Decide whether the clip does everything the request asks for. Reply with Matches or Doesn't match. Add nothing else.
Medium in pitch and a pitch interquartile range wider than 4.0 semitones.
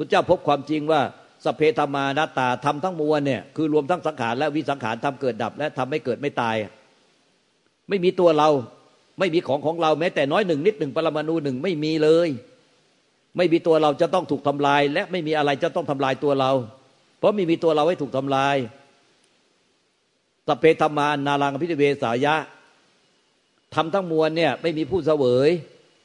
Doesn't match